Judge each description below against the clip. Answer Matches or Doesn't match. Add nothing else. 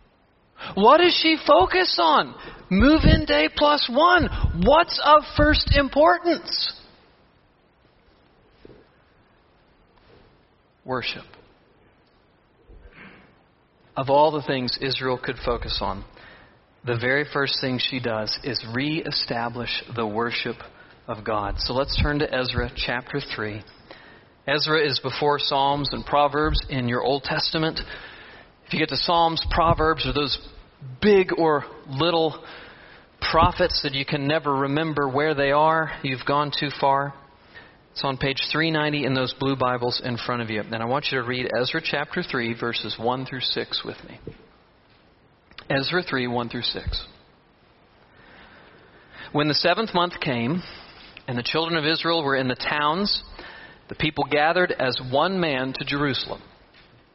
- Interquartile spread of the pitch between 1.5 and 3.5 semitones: Doesn't match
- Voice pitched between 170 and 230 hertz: Doesn't match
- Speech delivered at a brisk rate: Doesn't match